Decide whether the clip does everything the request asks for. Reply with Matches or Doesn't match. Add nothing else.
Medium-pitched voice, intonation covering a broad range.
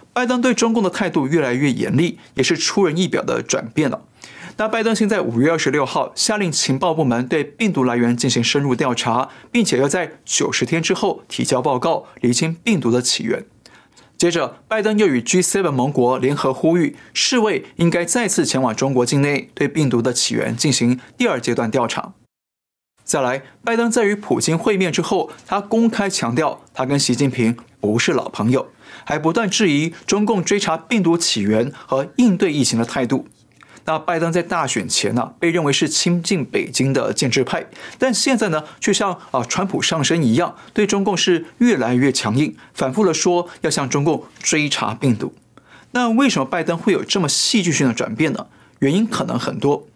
Matches